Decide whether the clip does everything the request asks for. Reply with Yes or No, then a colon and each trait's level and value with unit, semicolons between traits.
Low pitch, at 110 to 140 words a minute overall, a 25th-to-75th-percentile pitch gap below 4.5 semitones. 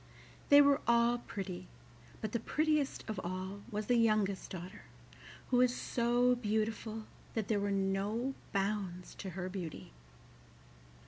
No: high, 215 Hz; slow, 135 wpm; average, 3.8 semitones